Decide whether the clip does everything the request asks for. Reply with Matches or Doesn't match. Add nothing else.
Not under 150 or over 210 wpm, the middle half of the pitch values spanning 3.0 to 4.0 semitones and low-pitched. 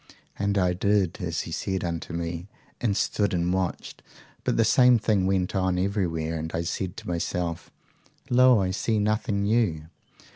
Matches